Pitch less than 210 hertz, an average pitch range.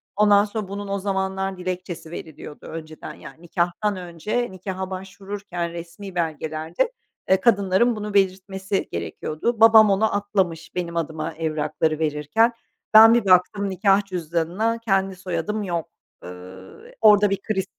Yes: high, 190 Hz; average, 3.3 semitones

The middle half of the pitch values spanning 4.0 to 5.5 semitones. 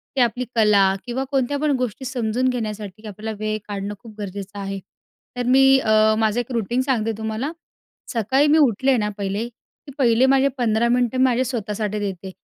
No: average, 3.5 semitones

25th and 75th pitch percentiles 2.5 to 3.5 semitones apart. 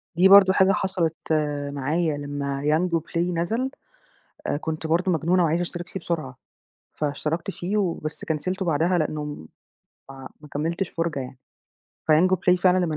Yes: average, 3.1 semitones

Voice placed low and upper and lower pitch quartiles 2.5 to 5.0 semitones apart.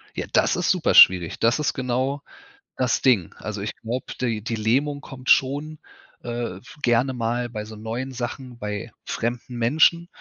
Yes: low, 120 Hz; average, 2.8 semitones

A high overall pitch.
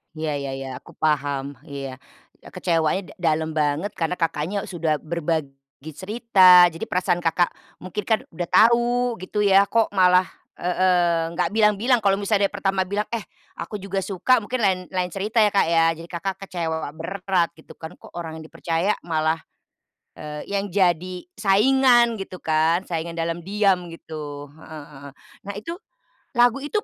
No: medium, 180 Hz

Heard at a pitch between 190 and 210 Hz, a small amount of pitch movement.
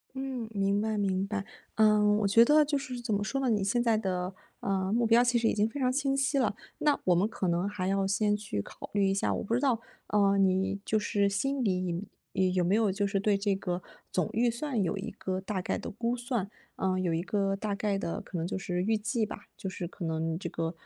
No: high, 205 Hz; average, 3.4 semitones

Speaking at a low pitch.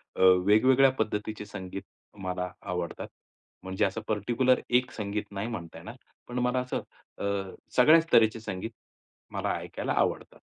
Yes: low, 105 Hz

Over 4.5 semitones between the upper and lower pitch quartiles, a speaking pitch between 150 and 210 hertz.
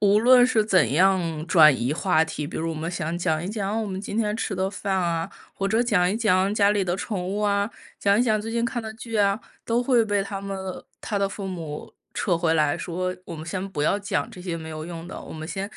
No: average, 3.8 semitones; high, 190 Hz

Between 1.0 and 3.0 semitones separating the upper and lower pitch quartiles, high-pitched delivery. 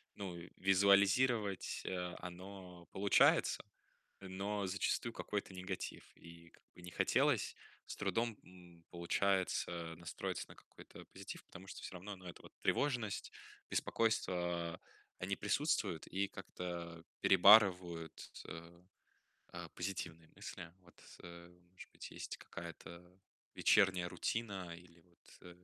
No: narrow, 2.4 semitones; very low, 90 Hz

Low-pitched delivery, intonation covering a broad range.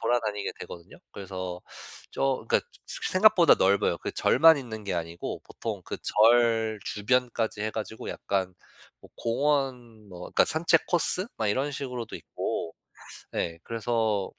No: low, 115 Hz; average, 4.6 semitones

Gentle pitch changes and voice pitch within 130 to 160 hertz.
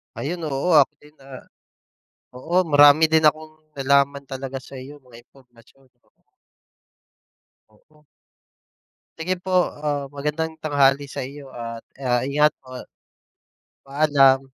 Yes: narrow, 2.3 semitones; medium, 140 Hz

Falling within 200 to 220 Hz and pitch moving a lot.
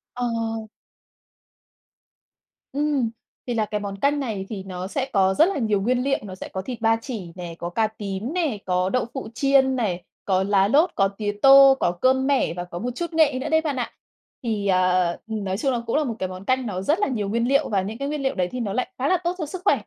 No: high, 230 Hz; wide, 5.9 semitones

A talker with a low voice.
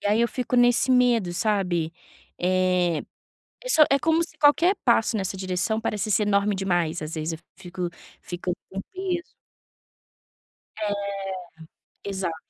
No: high, 200 Hz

